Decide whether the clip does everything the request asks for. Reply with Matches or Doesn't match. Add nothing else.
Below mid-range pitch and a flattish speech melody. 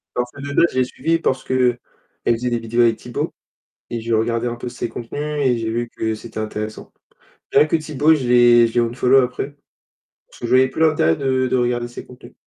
Matches